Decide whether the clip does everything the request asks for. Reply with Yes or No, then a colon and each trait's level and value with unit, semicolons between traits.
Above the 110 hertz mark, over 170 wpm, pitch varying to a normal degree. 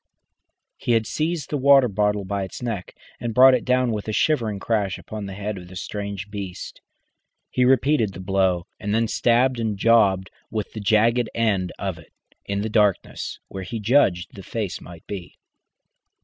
No: low, 105 Hz; average, 180 wpm; average, 3.3 semitones